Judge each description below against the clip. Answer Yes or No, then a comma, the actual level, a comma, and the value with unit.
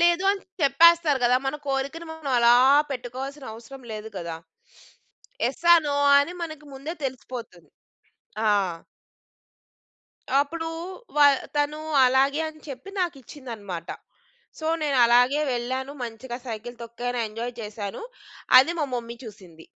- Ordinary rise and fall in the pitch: Yes, average, 3.9 semitones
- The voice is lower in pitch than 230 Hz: No, very high, 260 Hz